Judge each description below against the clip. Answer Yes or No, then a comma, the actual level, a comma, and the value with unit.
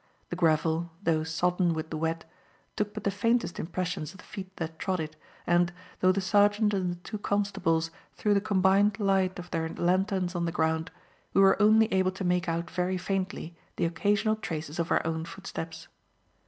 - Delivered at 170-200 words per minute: Yes, average, 190 wpm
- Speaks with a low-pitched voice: No, medium, 180 Hz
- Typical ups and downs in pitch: Yes, average, 3.0 semitones